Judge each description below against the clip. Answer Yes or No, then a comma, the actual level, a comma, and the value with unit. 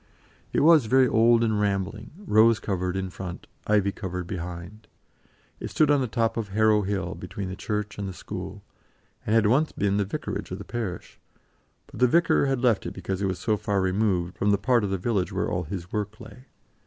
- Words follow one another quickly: Yes, fast, 210 wpm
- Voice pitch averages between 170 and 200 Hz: No, low, 105 Hz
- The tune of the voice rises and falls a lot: No, average, 3.2 semitones